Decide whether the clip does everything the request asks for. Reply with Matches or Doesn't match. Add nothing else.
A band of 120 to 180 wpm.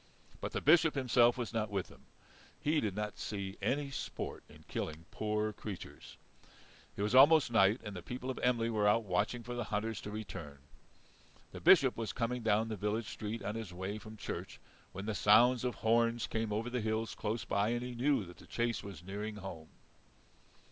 Doesn't match